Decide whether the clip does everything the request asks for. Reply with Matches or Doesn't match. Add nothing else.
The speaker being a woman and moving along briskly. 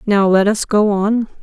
Matches